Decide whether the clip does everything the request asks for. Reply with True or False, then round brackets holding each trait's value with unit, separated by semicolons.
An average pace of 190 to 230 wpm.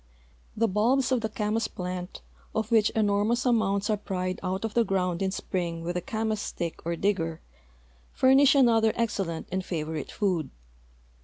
False (160 wpm)